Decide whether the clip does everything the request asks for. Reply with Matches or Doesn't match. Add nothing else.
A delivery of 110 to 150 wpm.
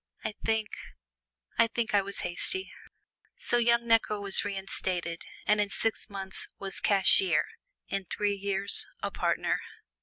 Matches